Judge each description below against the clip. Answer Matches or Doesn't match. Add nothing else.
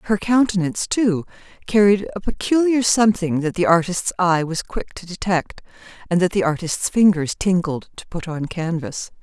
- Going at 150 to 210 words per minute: Matches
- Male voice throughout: Doesn't match